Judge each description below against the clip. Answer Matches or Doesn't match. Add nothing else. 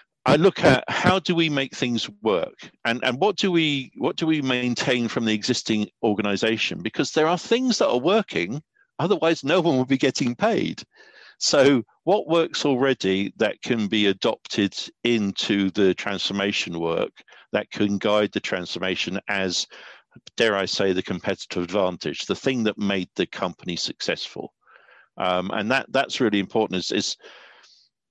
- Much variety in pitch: Matches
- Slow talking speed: Doesn't match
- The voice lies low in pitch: Matches